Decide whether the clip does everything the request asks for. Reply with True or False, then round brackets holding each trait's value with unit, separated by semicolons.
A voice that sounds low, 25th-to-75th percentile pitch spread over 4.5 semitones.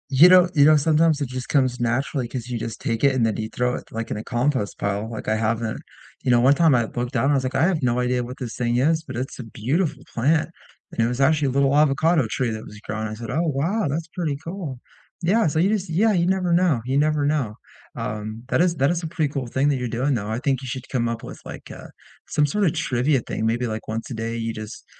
True (130 Hz; 4.9 semitones)